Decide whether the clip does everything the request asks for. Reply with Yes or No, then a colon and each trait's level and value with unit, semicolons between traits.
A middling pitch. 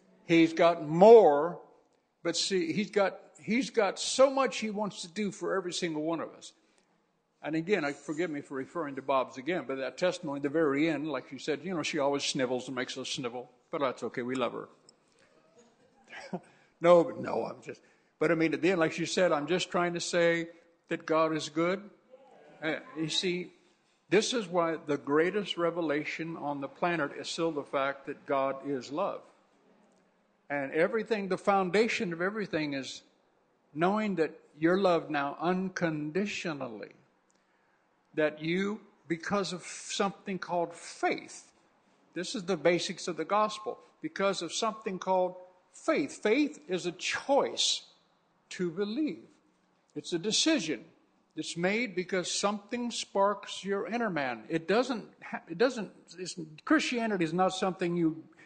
Yes: medium, 175 Hz